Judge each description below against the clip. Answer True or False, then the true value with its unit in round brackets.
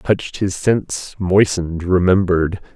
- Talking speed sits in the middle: False (110 wpm)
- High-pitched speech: False (90 Hz)